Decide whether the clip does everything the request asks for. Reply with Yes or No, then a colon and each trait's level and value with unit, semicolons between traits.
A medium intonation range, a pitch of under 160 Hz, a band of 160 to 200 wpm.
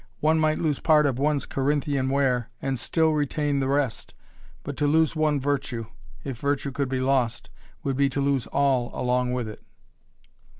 No: narrow, 2.2 semitones; medium, 140 Hz; average, 175 wpm